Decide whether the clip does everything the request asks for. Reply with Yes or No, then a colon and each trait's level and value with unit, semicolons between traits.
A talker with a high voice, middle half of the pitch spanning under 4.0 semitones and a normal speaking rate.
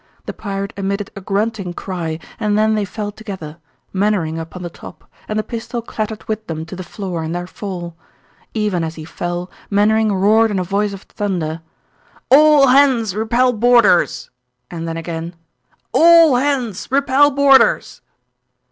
No: high, 205 Hz; average, 4.3 semitones; average, 155 wpm